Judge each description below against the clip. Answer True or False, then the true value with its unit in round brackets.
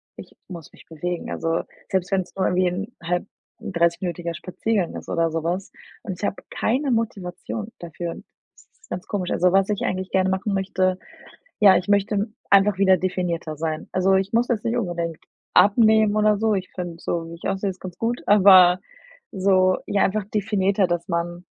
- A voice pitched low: False (185 Hz)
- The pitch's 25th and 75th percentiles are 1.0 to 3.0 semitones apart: True (2.6 semitones)